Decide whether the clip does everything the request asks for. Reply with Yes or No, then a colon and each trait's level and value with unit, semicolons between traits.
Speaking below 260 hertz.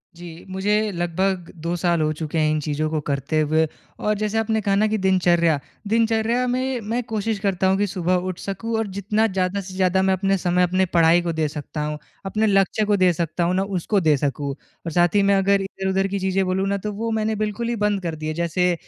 Yes: high, 190 Hz